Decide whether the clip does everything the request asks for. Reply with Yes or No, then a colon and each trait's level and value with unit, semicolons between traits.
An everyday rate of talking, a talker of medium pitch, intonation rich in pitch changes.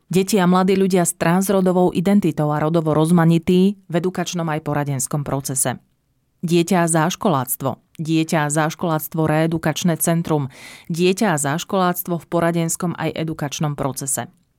No: average, 130 wpm; medium, 165 Hz; average, 2.8 semitones